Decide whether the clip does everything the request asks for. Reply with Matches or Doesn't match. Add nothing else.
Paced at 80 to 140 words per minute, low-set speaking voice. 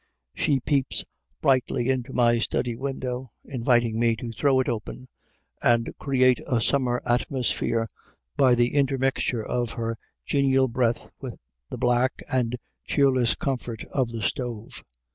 Matches